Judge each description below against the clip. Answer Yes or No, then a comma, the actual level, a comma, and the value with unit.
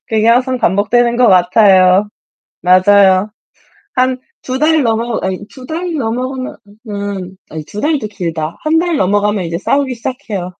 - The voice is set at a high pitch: Yes, high, 215 Hz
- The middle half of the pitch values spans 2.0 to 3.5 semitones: No, average, 5.3 semitones